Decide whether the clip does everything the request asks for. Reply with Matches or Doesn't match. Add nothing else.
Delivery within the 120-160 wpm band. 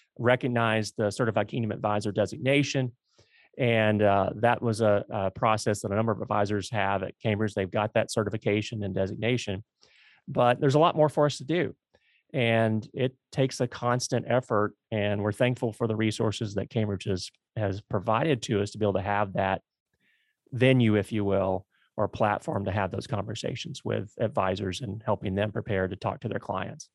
Doesn't match